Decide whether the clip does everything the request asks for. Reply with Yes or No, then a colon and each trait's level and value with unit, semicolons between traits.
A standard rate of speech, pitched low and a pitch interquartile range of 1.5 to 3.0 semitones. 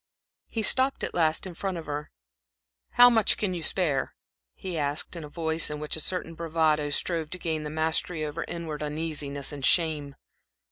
No: average, 185 wpm; medium, 160 Hz; narrow, 2.5 semitones